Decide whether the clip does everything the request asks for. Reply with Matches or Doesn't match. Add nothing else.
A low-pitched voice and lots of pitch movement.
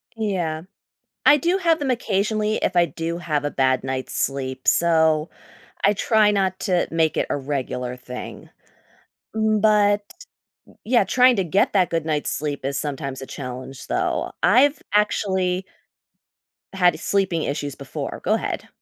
Doesn't match